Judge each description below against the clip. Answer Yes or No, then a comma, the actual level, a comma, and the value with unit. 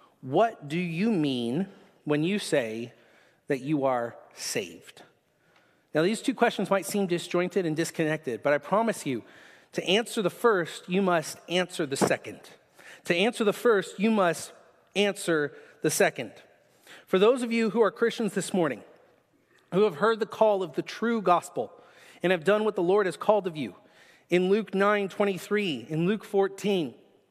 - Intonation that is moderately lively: Yes, average, 3.9 semitones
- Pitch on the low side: No, high, 190 Hz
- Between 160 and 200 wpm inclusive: Yes, average, 165 wpm